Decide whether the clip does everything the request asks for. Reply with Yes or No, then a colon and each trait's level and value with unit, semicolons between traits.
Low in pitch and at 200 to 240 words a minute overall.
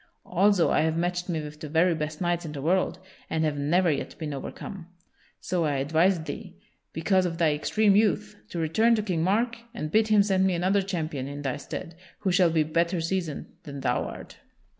No: medium, 170 Hz; fast, 205 wpm